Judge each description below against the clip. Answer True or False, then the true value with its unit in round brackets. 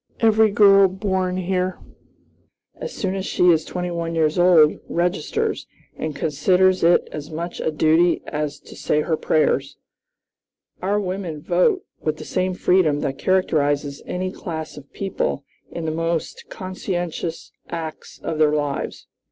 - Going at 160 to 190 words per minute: False (145 wpm)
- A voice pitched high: False (170 Hz)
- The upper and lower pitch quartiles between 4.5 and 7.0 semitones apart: False (3.2 semitones)